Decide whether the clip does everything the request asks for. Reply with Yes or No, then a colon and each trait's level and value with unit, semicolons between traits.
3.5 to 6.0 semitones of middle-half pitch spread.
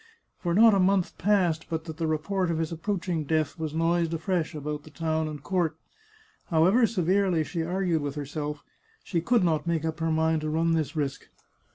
No: narrow, 2.4 semitones